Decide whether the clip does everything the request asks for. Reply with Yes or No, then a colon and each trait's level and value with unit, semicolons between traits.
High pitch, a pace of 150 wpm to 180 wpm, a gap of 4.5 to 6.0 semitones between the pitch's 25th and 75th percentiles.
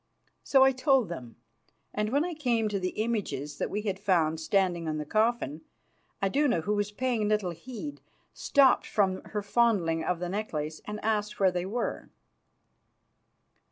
Yes: high, 205 Hz; average, 160 wpm; average, 5.2 semitones